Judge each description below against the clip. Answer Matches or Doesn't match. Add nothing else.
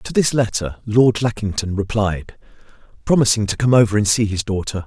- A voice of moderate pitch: Doesn't match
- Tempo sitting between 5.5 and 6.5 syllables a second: Doesn't match